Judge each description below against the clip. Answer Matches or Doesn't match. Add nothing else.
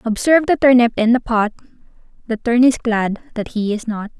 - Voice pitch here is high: Matches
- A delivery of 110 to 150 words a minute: Doesn't match